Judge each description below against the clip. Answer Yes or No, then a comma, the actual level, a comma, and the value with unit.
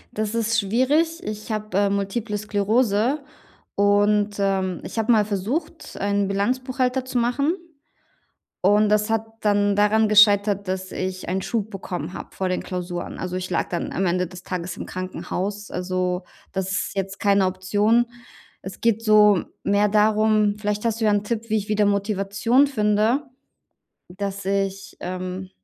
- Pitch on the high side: Yes, high, 205 Hz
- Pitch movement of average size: No, narrow, 2.2 semitones